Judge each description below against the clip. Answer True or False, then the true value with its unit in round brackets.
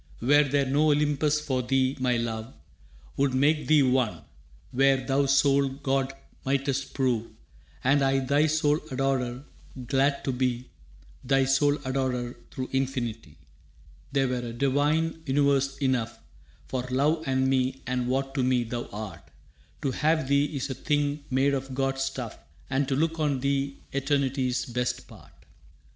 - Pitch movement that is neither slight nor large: False (1.7 semitones)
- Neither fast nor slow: True (150 wpm)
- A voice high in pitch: False (135 Hz)